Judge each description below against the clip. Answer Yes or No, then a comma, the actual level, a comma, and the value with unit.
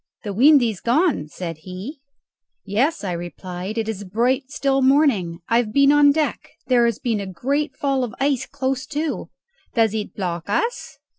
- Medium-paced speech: Yes, average, 180 wpm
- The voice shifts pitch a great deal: Yes, wide, 5.9 semitones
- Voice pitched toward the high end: Yes, high, 240 Hz